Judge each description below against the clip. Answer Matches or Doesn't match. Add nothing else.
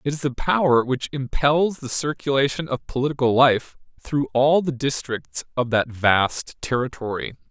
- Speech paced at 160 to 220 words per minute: Doesn't match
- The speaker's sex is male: Matches